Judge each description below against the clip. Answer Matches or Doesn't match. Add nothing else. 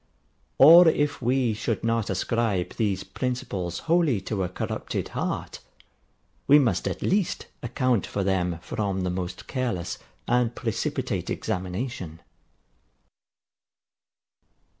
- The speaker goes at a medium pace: Doesn't match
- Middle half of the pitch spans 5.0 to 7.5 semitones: Matches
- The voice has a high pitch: Doesn't match